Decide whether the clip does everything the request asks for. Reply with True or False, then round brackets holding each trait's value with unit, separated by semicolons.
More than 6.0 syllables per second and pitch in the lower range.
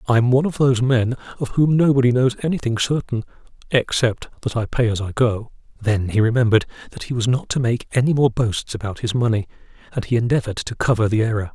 True (6.2 syllables/s; 120 Hz)